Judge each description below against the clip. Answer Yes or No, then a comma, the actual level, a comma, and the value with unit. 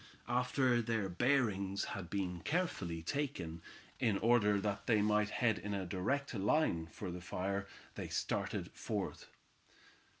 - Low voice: Yes, low, 105 Hz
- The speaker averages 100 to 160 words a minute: Yes, slow, 135 wpm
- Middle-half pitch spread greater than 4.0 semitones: Yes, average, 4.4 semitones